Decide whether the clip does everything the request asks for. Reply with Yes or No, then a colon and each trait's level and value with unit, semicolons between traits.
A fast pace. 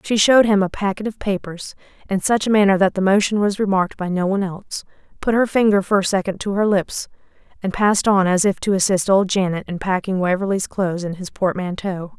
Yes: fast, 220 wpm